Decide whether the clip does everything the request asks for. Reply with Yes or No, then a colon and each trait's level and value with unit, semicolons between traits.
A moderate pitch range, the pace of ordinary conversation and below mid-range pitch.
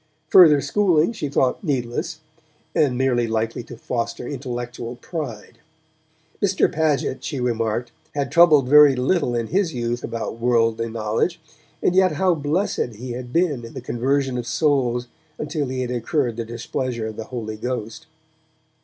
Yes: average, 4.1 semitones; average, 155 wpm; low, 125 Hz